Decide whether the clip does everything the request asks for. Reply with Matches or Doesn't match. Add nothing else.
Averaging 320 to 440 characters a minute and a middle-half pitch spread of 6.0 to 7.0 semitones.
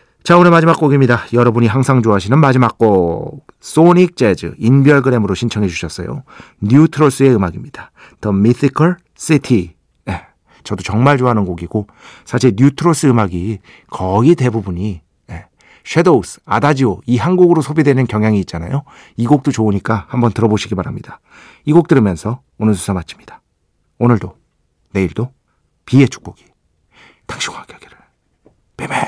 Doesn't match